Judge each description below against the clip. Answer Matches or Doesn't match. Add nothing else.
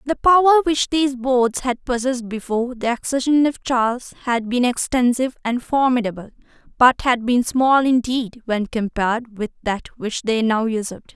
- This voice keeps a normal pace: Matches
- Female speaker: Matches